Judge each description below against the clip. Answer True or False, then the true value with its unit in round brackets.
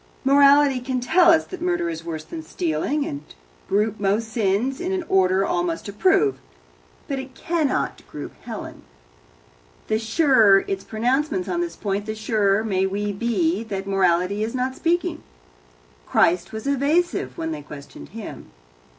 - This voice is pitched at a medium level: False (220 Hz)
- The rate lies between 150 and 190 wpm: True (155 wpm)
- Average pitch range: False (6.8 semitones)